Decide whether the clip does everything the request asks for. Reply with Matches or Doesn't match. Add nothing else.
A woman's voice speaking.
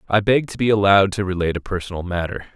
Doesn't match